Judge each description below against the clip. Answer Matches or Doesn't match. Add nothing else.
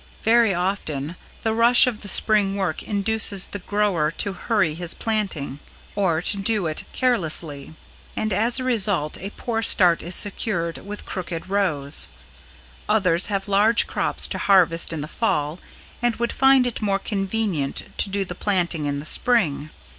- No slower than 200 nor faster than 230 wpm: Doesn't match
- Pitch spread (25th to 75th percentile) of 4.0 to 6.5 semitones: Matches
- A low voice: Doesn't match